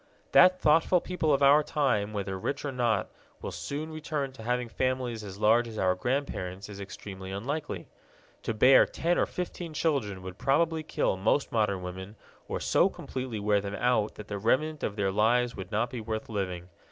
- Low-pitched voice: Yes, low, 115 Hz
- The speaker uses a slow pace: No, average, 190 wpm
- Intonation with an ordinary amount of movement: No, wide, 6.0 semitones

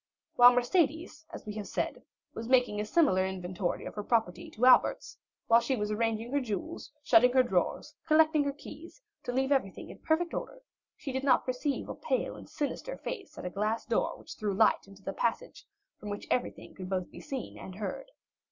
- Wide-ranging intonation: Yes, wide, 5.7 semitones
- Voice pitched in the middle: No, high, 245 Hz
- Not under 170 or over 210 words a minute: Yes, average, 200 wpm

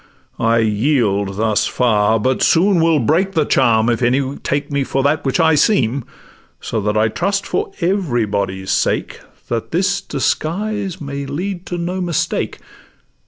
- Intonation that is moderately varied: No, wide, 7.5 semitones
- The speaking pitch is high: No, medium, 140 Hz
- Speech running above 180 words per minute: No, average, 155 wpm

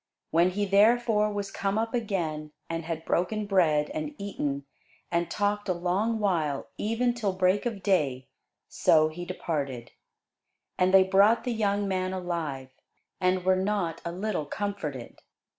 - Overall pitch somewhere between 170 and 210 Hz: Yes, medium, 185 Hz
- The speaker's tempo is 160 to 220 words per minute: No, average, 150 wpm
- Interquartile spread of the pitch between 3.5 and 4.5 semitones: Yes, average, 3.9 semitones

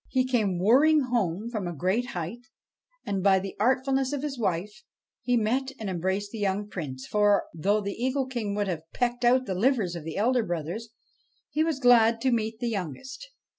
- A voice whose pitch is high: Yes, high, 220 Hz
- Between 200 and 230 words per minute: Yes, fast, 205 wpm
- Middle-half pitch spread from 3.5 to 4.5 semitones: No, average, 5.0 semitones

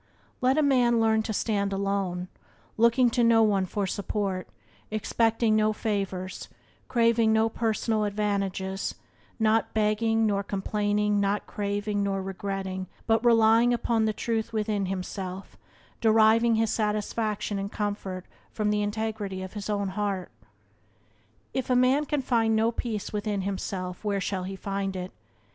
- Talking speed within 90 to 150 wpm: Yes, average, 145 wpm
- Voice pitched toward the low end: No, high, 210 Hz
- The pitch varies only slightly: Yes, narrow, 2.2 semitones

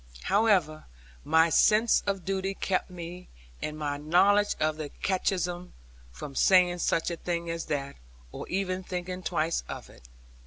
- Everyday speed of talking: Yes, average, 150 wpm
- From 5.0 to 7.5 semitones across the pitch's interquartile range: No, average, 3.1 semitones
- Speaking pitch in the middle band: Yes, medium, 180 Hz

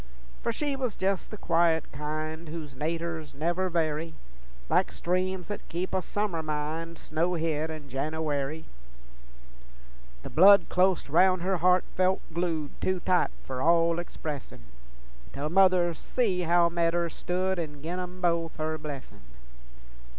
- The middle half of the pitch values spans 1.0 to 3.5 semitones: Yes, average, 2.8 semitones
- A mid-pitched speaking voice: Yes, medium, 170 Hz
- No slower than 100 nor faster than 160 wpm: Yes, slow, 135 wpm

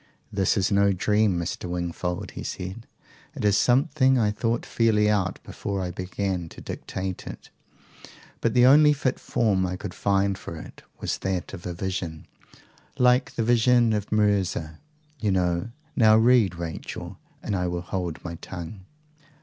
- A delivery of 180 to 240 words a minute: No, average, 160 wpm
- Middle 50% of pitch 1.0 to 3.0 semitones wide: No, average, 4.0 semitones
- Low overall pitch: Yes, low, 100 Hz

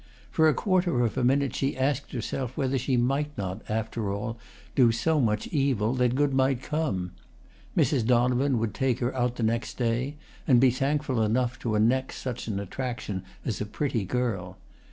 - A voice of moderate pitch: No, low, 125 Hz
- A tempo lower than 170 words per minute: No, average, 180 wpm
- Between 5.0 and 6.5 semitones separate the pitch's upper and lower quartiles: No, average, 3.1 semitones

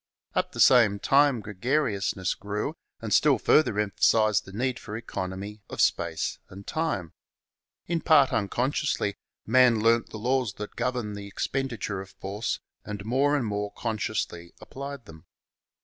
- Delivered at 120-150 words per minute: Yes, average, 145 wpm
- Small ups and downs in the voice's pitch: No, average, 4.3 semitones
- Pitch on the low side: Yes, low, 110 Hz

